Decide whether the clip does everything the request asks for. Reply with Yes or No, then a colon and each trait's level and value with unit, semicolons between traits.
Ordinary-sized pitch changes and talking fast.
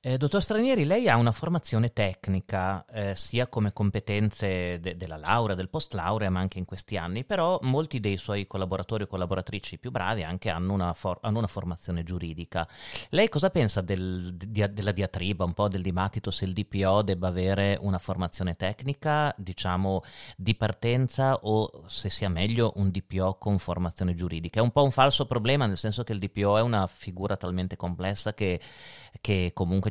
Yes: average, 3.3 semitones; fast, 180 wpm